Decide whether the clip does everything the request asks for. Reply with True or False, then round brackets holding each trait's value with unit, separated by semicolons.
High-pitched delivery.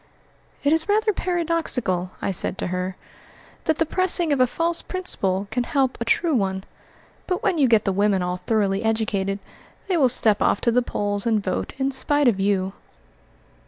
True (235 Hz)